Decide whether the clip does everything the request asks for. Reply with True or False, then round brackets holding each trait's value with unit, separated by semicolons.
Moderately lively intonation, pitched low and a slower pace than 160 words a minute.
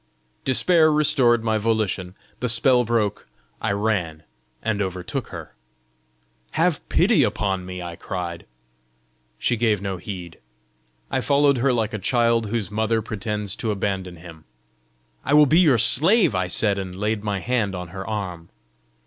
True (4.2 semitones; 105 Hz; 150 wpm)